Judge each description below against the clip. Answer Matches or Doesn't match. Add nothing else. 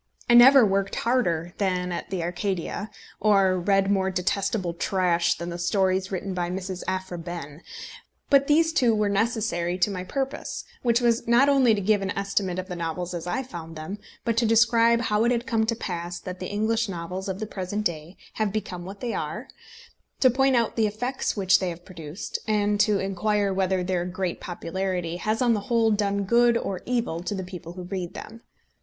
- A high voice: Matches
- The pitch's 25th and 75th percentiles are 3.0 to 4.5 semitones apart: Matches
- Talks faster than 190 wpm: Matches